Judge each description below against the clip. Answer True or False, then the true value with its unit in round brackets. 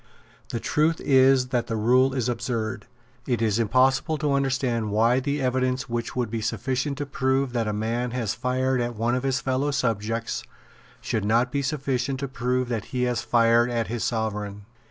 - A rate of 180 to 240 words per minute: True (185 wpm)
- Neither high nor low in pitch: False (125 Hz)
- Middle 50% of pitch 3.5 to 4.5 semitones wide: False (2.4 semitones)